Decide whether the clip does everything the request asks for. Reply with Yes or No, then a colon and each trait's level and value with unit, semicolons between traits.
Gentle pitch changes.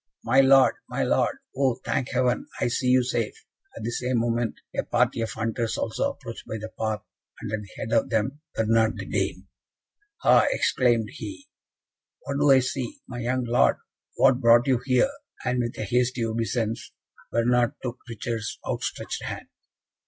Yes: narrow, 2.1 semitones